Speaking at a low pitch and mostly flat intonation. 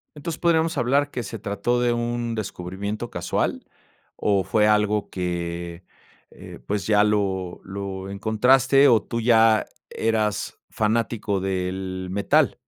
No: low, 105 Hz; average, 3.6 semitones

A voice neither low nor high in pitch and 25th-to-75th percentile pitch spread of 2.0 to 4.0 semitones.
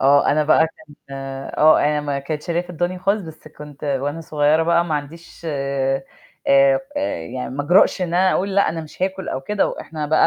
Yes: medium, 155 Hz; average, 3.7 semitones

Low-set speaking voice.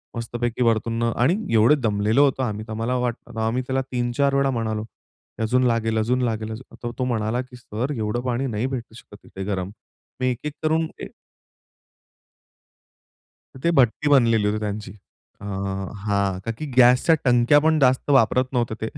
Yes: low, 120 Hz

